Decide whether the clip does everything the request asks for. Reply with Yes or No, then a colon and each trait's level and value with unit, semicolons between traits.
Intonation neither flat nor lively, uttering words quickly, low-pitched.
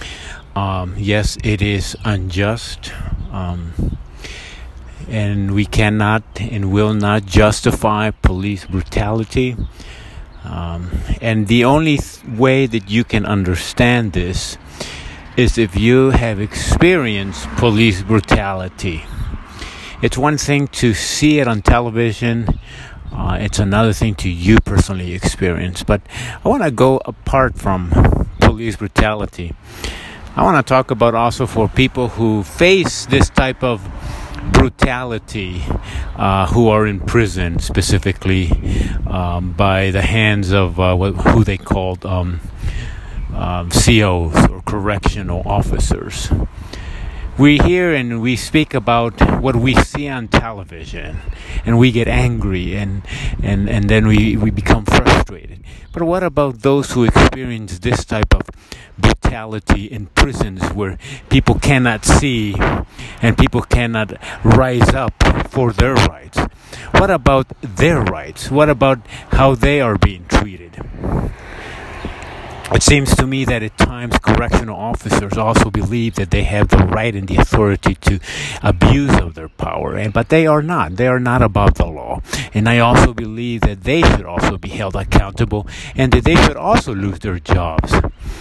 No: average, 4.4 semitones; average, 140 wpm; low, 105 Hz